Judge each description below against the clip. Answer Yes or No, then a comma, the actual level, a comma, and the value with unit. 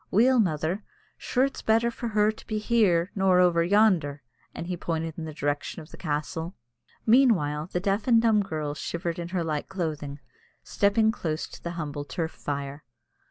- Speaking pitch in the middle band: Yes, medium, 175 Hz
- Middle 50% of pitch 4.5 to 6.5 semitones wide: Yes, wide, 5.4 semitones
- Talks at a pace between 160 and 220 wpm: Yes, average, 180 wpm